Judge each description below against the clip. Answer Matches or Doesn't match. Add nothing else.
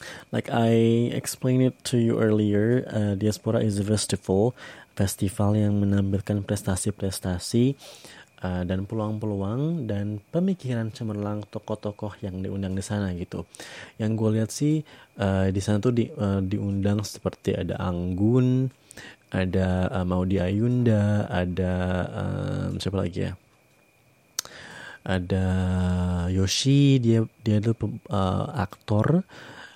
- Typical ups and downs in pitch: Matches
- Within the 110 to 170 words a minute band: Matches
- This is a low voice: Matches